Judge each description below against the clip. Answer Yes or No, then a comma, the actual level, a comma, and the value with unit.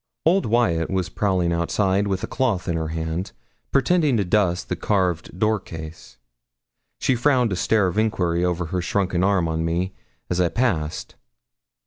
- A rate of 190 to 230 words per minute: No, average, 165 wpm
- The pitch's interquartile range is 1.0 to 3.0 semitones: No, average, 3.9 semitones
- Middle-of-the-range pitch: No, very low, 95 Hz